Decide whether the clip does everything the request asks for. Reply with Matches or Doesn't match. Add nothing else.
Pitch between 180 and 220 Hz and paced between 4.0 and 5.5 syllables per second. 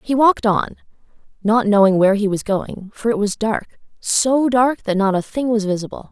Matches